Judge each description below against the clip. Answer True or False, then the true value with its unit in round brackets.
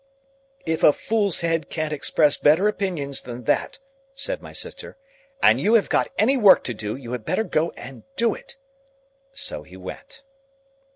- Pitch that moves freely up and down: True (8.2 semitones)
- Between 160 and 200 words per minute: True (170 wpm)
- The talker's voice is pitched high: False (165 Hz)